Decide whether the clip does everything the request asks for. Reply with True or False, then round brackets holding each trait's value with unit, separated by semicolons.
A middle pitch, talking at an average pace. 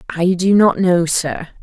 True (180 Hz; 185 wpm)